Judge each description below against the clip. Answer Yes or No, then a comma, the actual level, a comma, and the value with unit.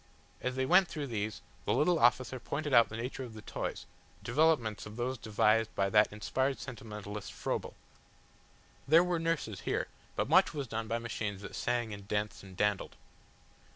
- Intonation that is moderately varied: Yes, average, 4.1 semitones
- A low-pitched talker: Yes, low, 115 Hz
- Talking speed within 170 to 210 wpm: Yes, average, 175 wpm